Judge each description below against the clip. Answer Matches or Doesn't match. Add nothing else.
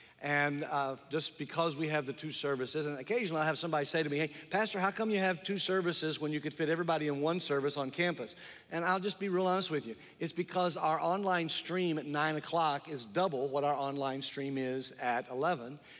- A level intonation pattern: Doesn't match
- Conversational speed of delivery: Doesn't match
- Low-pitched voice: Doesn't match